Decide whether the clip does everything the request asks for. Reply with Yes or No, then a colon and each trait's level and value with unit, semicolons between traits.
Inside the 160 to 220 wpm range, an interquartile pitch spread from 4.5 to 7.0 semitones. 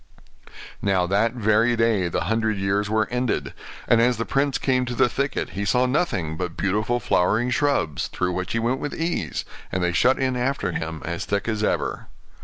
Yes: average, 195 wpm; average, 4.9 semitones